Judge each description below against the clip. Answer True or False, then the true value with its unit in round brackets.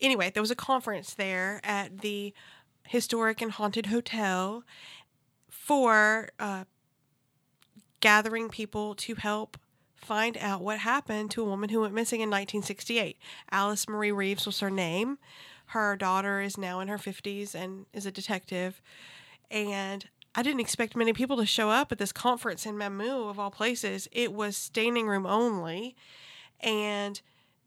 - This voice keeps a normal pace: True (150 wpm)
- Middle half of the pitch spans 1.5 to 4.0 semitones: True (2.4 semitones)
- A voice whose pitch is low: False (210 Hz)